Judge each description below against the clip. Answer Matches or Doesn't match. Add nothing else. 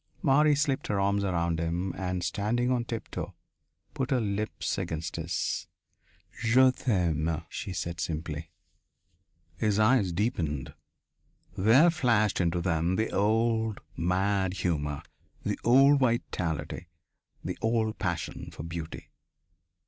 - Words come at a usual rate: Doesn't match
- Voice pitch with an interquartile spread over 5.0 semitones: Matches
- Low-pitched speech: Matches